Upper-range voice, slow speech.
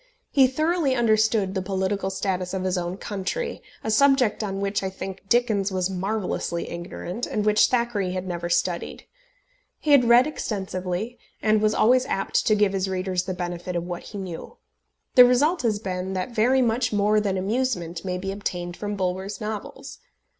No: high, 200 Hz; average, 175 wpm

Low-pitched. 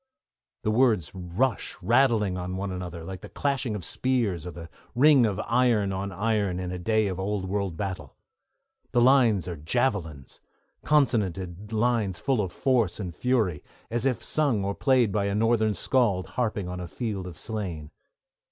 Yes: low, 100 Hz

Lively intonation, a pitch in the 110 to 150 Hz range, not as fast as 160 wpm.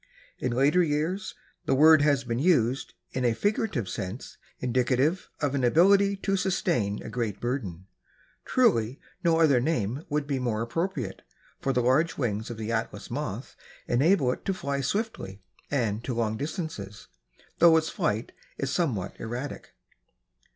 Yes: wide, 5.8 semitones; low, 135 Hz; average, 150 wpm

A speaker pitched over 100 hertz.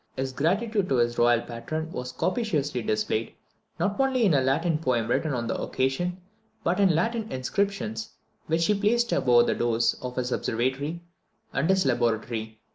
Yes: low, 135 Hz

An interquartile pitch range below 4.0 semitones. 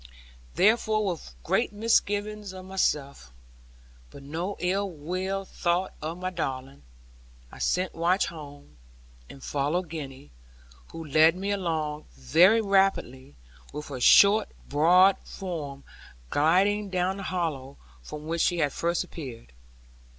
No: average, 4.8 semitones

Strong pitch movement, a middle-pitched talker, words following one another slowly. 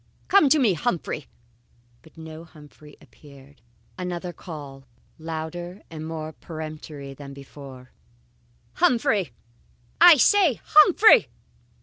Yes: wide, 5.7 semitones; medium, 160 Hz; slow, 100 wpm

